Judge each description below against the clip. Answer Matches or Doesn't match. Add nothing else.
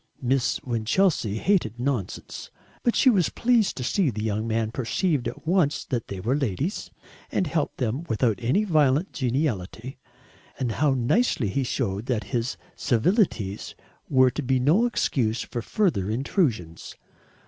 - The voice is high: Doesn't match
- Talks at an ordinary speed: Matches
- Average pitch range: Doesn't match